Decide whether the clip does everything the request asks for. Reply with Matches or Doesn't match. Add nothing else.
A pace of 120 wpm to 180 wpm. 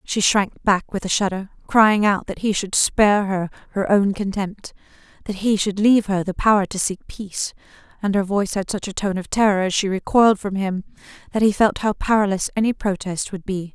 Doesn't match